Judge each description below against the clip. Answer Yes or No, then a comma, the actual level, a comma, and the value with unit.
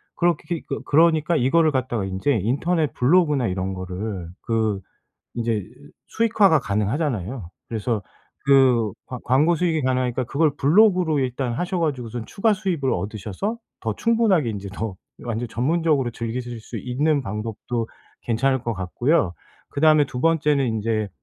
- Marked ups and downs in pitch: Yes, wide, 6.0 semitones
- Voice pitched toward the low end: Yes, low, 130 Hz